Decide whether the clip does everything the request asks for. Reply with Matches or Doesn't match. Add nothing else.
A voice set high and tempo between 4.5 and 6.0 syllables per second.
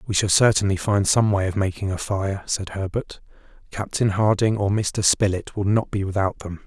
Doesn't match